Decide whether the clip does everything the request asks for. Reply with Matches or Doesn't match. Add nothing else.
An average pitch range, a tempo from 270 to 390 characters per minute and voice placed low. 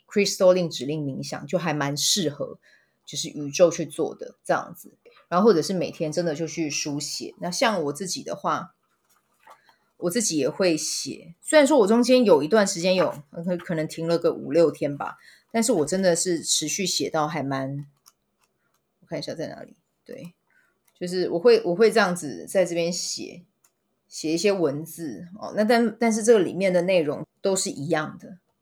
Doesn't match